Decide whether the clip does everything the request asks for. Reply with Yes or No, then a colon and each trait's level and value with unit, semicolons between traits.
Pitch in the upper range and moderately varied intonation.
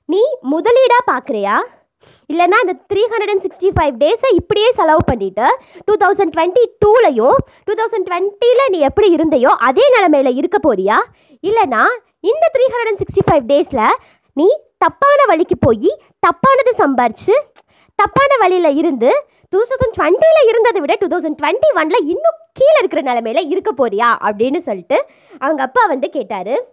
No: very high, 375 Hz; wide, 6.1 semitones